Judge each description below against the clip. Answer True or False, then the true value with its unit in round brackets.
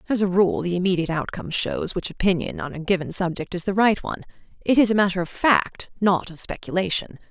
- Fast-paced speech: True (215 wpm)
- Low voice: False (190 Hz)